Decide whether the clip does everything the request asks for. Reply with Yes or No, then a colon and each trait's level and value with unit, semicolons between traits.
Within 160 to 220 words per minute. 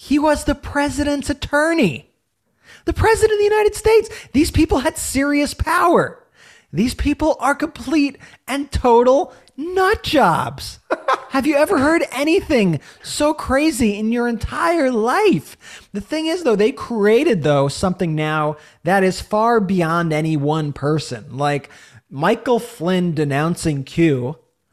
No: slow, 135 wpm